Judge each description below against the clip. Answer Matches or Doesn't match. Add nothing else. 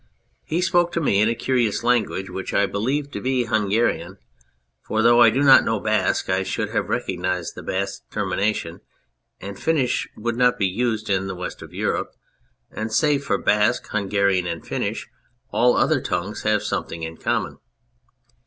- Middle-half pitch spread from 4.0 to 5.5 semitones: Matches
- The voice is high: Doesn't match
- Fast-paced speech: Doesn't match